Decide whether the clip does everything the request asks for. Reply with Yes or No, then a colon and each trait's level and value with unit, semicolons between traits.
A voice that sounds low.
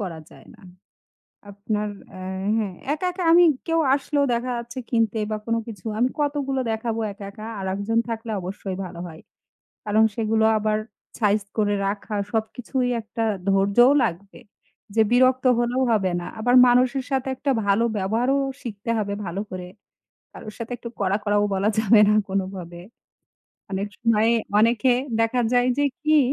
No: high, 220 Hz